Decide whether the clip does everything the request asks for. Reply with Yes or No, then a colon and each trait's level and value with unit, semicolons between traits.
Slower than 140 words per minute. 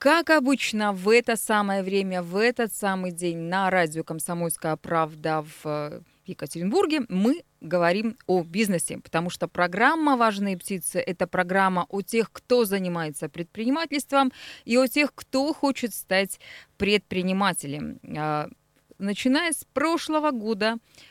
Yes: average, 120 wpm